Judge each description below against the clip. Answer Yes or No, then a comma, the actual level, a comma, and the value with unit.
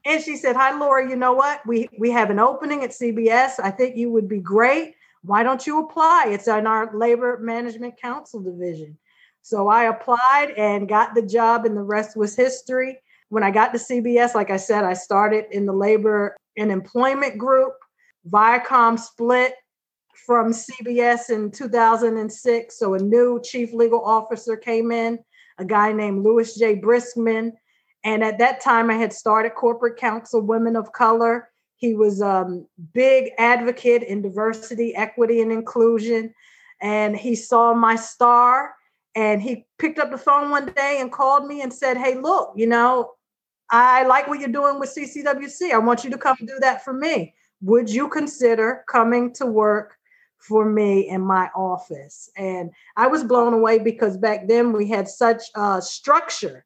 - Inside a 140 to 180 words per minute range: Yes, average, 175 wpm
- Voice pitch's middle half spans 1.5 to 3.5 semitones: Yes, average, 2.7 semitones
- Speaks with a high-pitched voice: Yes, high, 230 Hz